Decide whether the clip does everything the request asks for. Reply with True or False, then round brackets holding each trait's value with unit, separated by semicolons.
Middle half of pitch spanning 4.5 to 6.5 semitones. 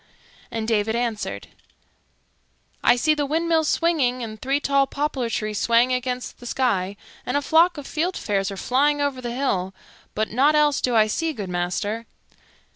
True (5.0 semitones)